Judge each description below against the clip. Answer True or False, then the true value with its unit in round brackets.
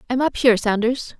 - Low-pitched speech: False (240 Hz)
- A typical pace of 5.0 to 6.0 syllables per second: False (6.2 syllables/s)